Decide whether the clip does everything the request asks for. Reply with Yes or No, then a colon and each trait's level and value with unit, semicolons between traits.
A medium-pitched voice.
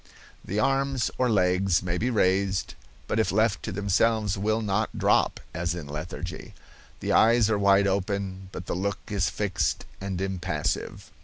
No: low, 100 Hz